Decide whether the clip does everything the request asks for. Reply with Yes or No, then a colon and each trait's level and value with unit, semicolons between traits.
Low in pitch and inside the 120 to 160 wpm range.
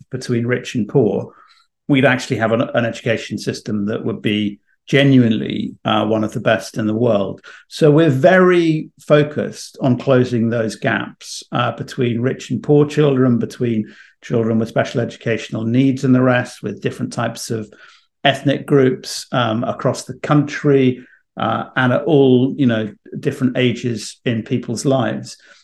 Yes: low, 125 Hz; average, 155 wpm